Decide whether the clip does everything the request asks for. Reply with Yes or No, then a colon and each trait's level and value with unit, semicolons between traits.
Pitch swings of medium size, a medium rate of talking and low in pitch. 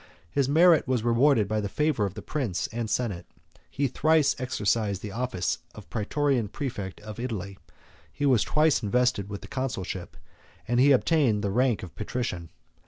Yes: average, 4.8 semitones; average, 170 wpm; low, 120 Hz